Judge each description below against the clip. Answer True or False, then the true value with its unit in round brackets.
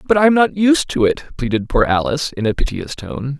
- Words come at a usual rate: False (230 wpm)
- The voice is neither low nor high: True (150 Hz)